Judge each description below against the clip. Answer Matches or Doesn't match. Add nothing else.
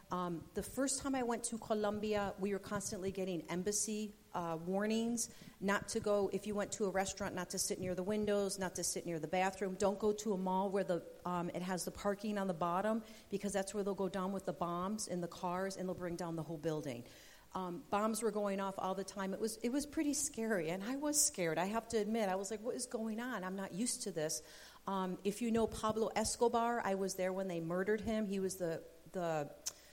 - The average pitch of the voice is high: Matches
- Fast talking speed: Matches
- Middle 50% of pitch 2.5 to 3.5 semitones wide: Matches